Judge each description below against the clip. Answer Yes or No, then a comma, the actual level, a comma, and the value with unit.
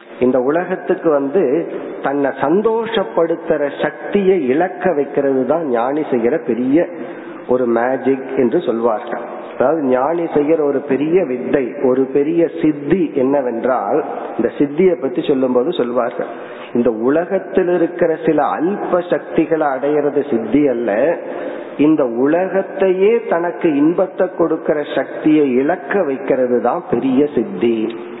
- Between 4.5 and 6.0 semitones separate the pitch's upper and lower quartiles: Yes, average, 5.3 semitones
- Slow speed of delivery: No, average, 110 wpm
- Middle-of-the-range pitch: Yes, medium, 150 Hz